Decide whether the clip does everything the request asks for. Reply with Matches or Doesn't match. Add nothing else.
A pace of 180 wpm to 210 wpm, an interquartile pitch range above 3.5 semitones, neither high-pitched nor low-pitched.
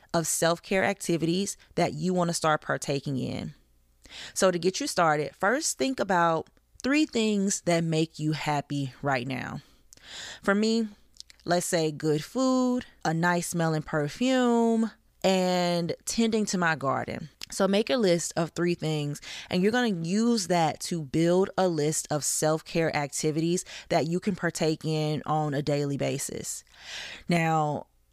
Doesn't match